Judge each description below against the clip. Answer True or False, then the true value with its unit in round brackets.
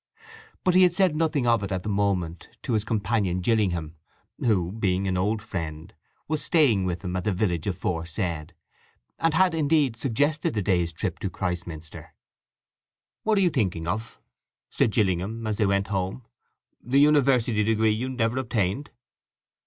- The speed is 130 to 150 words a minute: False (160 wpm)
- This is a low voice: True (105 Hz)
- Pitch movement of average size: False (5.9 semitones)